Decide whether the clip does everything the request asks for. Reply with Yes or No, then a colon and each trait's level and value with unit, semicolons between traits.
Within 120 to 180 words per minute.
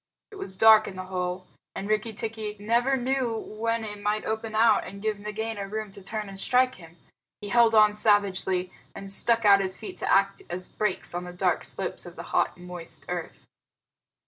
No: average, 200 wpm